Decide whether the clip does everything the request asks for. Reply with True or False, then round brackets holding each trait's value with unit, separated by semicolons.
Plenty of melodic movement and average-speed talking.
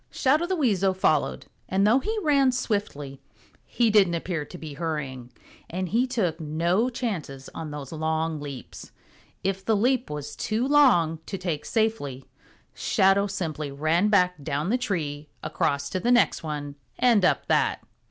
True (6.8 semitones; 160 wpm)